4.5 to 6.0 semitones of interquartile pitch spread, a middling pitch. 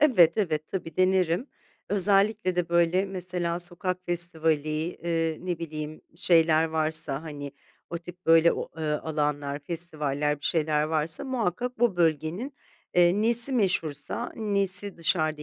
No: average, 3.1 semitones; medium, 170 Hz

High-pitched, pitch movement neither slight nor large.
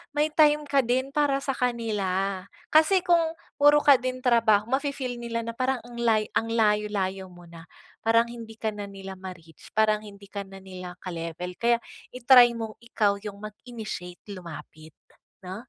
Yes: high, 225 Hz; average, 4.7 semitones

